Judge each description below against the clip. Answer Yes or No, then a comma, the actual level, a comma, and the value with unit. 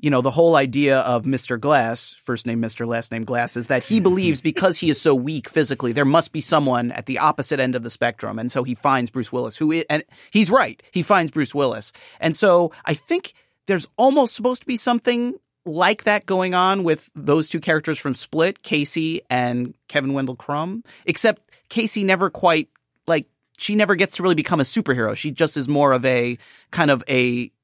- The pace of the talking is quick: Yes, fast, 210 wpm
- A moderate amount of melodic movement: No, wide, 6.4 semitones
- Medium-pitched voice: Yes, medium, 150 Hz